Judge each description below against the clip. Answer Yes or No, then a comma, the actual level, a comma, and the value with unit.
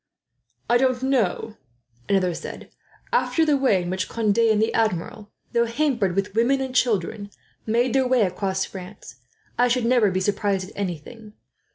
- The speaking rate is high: No, average, 165 wpm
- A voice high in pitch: Yes, high, 220 Hz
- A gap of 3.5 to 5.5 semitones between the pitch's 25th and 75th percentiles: Yes, average, 4.3 semitones